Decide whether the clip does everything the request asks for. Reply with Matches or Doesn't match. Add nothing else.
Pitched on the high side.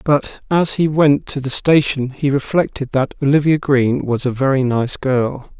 Doesn't match